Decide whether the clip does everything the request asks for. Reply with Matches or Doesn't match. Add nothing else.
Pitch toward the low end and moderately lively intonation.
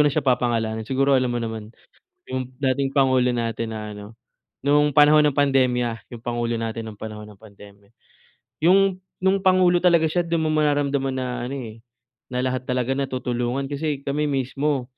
Matches